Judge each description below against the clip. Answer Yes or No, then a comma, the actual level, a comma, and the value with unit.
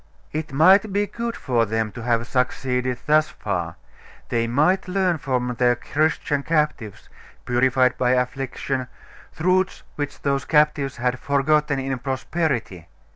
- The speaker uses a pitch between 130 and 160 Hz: Yes, low, 135 Hz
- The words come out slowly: Yes, slow, 130 wpm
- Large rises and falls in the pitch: No, average, 3.8 semitones